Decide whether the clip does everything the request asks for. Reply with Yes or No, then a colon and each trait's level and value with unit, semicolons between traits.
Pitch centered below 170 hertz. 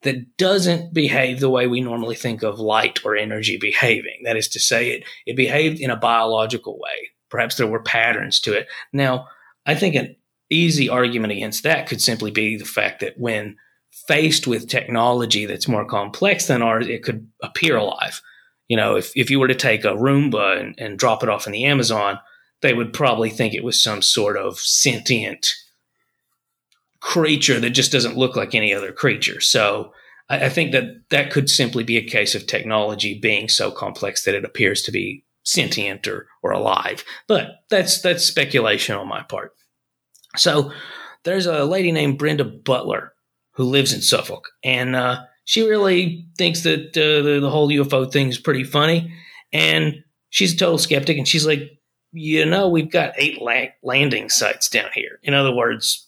Yes: low, 135 Hz